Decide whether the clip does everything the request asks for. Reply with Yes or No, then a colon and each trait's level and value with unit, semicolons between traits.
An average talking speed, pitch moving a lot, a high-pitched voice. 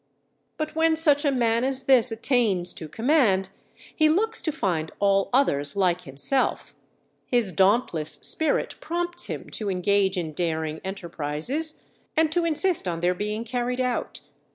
Yes: average, 155 wpm; wide, 8.2 semitones; high, 225 Hz